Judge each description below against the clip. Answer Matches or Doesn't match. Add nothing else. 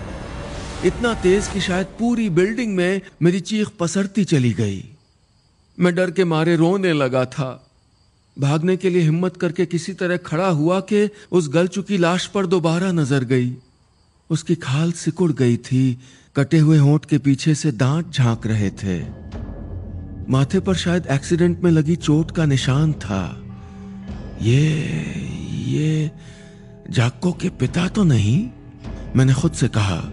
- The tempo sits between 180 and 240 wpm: Doesn't match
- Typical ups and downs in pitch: Doesn't match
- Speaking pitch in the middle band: Matches